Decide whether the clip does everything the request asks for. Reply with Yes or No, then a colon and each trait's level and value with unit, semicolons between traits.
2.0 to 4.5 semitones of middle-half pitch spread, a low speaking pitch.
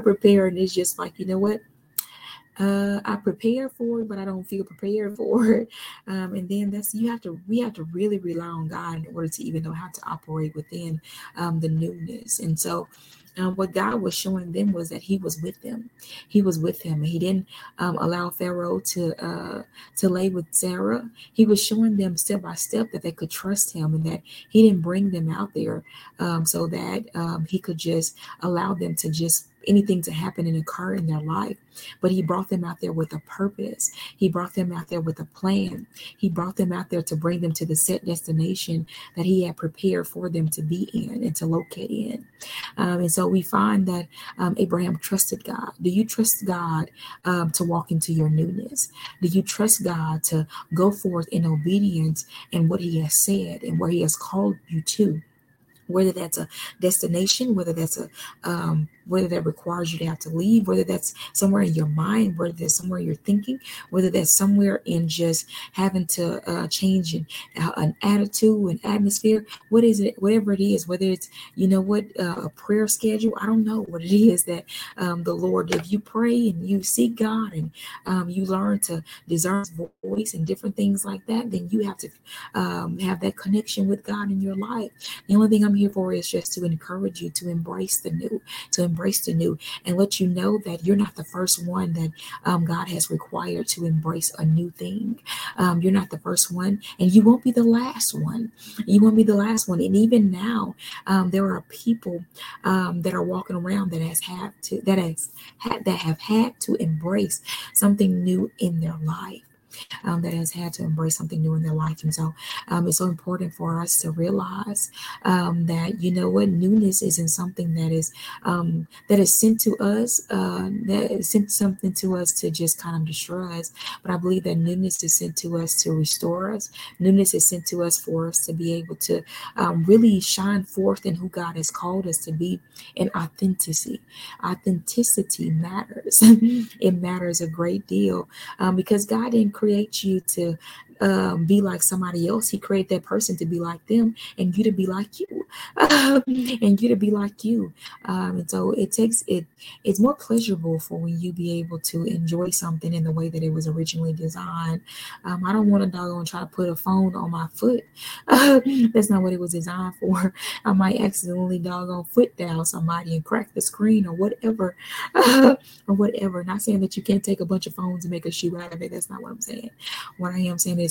No: average, 3.4 semitones; medium, 185 Hz